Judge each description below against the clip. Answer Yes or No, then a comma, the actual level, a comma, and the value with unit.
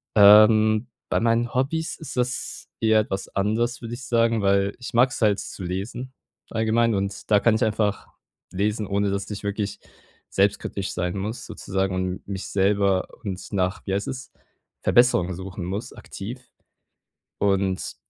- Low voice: Yes, low, 105 Hz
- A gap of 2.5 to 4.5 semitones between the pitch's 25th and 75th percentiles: Yes, average, 2.9 semitones